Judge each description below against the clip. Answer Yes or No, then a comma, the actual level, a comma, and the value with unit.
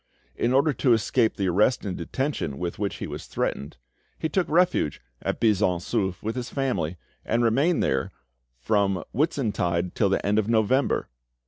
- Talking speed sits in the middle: Yes, average, 165 wpm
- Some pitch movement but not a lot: No, wide, 6.1 semitones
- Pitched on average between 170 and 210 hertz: No, low, 110 Hz